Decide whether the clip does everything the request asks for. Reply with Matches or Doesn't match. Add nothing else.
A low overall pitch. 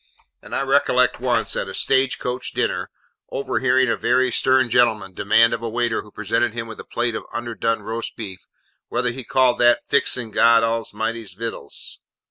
Matches